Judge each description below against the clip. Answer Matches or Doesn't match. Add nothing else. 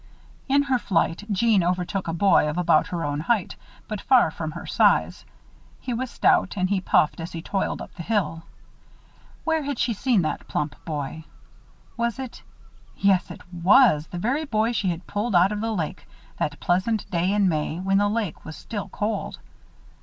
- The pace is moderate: Matches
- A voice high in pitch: Matches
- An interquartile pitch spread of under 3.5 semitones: Doesn't match